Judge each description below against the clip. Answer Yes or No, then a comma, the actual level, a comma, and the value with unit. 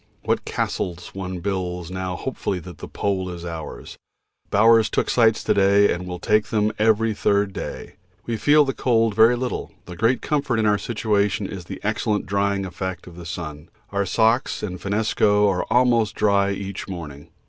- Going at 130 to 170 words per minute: No, average, 180 wpm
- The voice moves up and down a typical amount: Yes, average, 3.4 semitones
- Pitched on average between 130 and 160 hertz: No, low, 100 Hz